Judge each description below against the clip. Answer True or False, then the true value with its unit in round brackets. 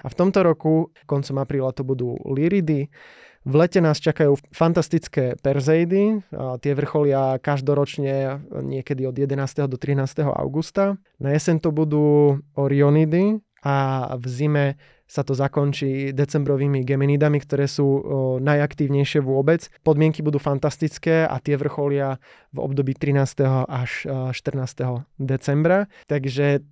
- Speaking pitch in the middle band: True (145 Hz)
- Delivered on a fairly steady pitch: True (2.2 semitones)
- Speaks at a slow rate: False (120 wpm)